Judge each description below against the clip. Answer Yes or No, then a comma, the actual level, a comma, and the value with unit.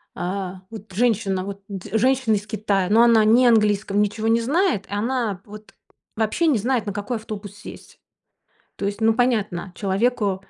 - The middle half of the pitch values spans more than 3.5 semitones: No, average, 2.7 semitones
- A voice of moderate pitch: No, high, 215 Hz